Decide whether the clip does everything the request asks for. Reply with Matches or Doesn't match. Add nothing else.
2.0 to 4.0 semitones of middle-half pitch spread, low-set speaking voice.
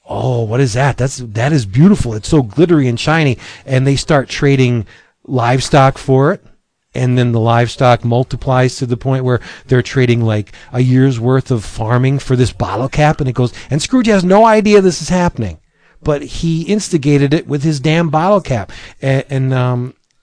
Matches